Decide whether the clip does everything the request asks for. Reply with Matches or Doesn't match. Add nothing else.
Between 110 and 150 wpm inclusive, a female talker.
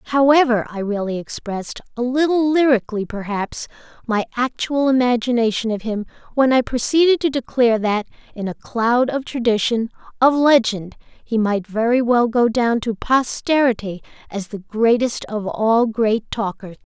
Matches